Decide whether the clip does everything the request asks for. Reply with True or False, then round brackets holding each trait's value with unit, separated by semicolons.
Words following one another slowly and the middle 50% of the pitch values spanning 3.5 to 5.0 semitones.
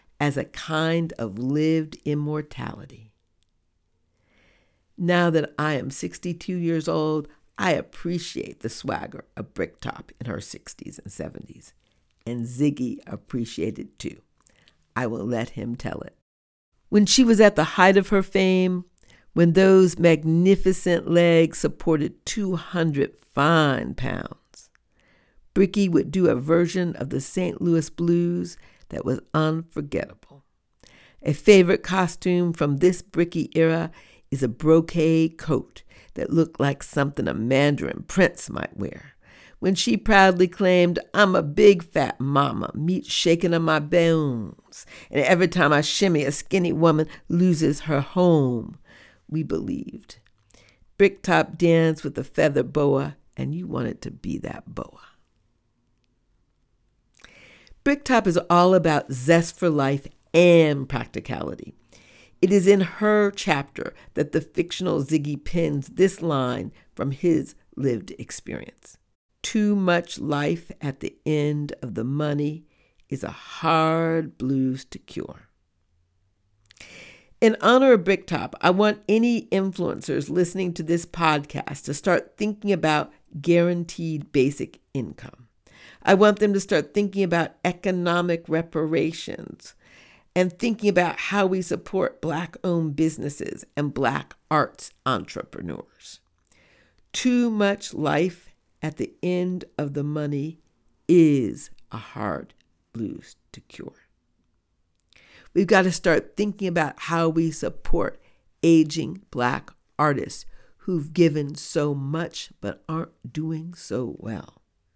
True (125 wpm; 4.4 semitones)